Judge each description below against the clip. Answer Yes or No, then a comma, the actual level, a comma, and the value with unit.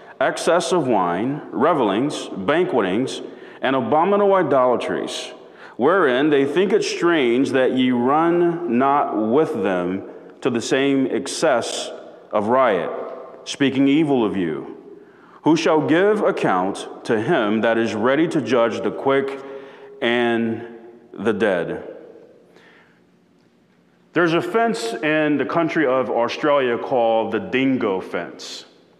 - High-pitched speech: No, low, 135 Hz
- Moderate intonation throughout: No, wide, 6.6 semitones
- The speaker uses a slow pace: Yes, slow, 120 wpm